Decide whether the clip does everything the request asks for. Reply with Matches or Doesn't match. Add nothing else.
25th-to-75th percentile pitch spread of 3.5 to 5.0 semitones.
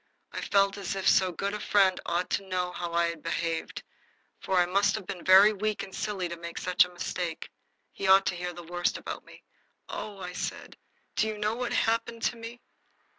Doesn't match